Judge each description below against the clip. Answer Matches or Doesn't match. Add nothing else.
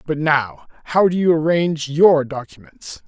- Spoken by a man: Matches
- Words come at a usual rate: Matches